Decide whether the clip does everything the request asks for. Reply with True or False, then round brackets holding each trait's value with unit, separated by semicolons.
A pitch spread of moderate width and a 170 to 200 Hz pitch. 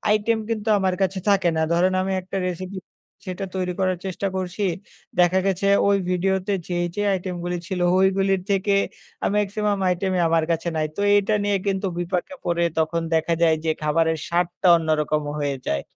False (2.3 semitones; 185 Hz)